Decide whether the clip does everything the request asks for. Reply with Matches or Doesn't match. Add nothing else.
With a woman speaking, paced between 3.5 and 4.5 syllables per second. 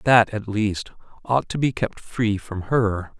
Doesn't match